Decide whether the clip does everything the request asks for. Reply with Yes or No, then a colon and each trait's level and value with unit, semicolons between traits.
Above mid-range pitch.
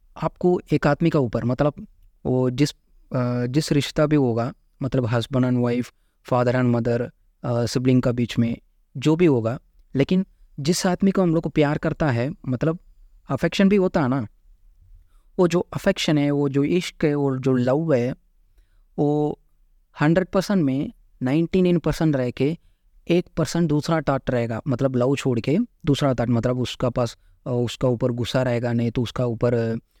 No: low, 135 Hz